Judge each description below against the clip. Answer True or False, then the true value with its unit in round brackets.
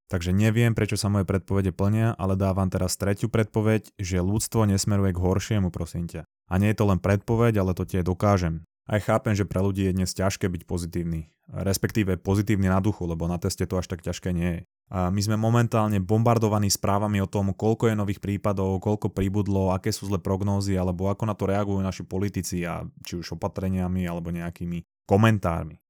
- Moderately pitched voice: False (95 Hz)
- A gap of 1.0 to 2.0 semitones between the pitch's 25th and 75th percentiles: False (2.4 semitones)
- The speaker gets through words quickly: True (195 wpm)